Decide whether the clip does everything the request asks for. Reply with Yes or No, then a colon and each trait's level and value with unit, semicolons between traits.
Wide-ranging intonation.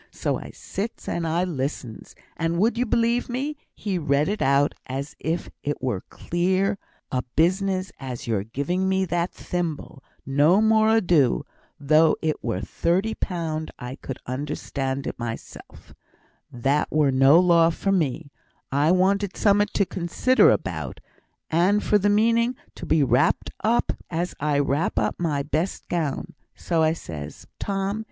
Yes: wide, 5.7 semitones